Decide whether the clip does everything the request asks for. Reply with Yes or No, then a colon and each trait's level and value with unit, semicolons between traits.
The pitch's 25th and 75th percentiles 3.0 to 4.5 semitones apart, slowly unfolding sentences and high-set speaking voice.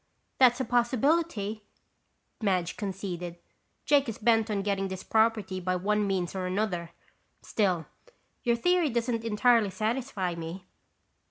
Yes: average, 4.0 semitones; slow, 125 wpm; high, 210 Hz